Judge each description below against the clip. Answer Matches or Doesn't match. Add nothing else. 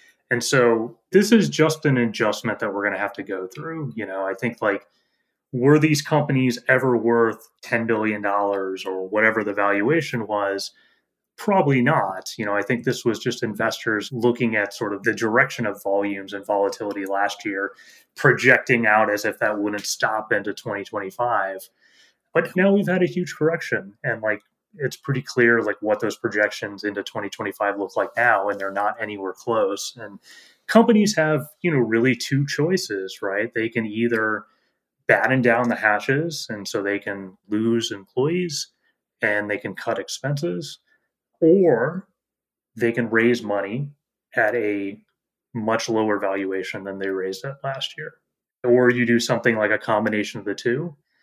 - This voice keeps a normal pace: Matches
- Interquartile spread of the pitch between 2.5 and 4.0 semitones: Doesn't match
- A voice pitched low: Matches